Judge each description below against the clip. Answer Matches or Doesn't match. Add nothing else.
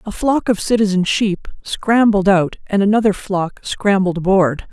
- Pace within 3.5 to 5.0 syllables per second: Matches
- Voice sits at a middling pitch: Doesn't match